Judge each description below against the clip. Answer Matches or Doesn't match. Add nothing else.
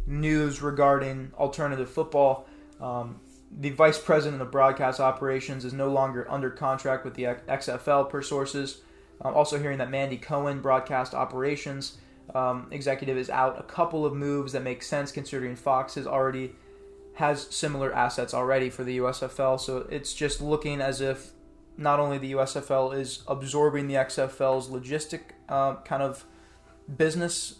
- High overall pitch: Doesn't match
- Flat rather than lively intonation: Matches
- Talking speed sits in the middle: Matches